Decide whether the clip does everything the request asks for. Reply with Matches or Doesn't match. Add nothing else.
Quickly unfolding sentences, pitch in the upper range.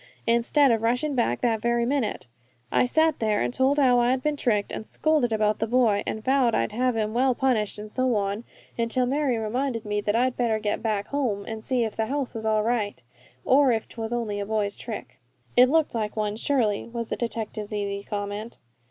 Matches